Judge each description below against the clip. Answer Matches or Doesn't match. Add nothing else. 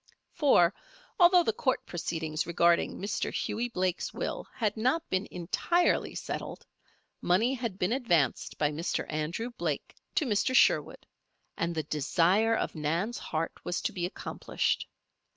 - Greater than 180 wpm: Doesn't match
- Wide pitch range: Matches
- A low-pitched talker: Doesn't match